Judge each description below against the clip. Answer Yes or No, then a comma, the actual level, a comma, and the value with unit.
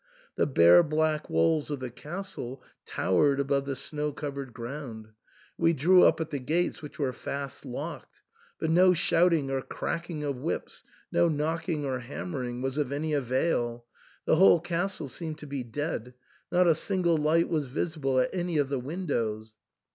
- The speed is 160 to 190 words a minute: Yes, average, 170 wpm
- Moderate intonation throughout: Yes, average, 4.1 semitones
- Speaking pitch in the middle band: Yes, medium, 145 Hz